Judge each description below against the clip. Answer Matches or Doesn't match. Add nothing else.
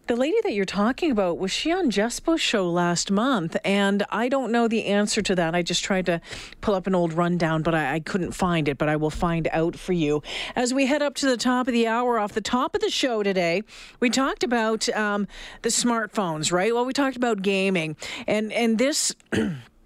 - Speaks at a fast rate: Matches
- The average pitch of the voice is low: Doesn't match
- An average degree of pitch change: Doesn't match